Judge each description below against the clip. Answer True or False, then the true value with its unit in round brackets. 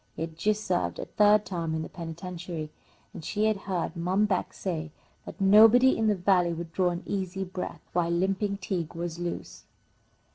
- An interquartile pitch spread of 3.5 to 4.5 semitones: False (2.9 semitones)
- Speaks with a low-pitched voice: False (180 Hz)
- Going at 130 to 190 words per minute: True (185 wpm)